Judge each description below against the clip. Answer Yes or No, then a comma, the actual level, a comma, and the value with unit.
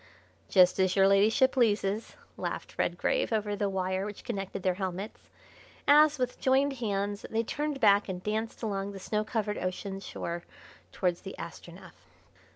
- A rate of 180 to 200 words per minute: No, average, 155 wpm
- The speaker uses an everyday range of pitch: Yes, average, 3.0 semitones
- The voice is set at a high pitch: Yes, high, 205 Hz